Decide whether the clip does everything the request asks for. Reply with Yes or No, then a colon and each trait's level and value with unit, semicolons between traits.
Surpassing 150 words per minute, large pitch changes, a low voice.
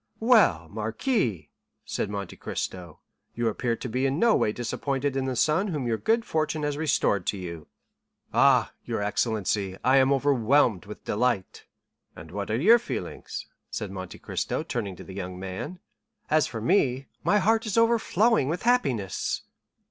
Yes: average, 165 wpm; wide, 7.4 semitones; low, 125 Hz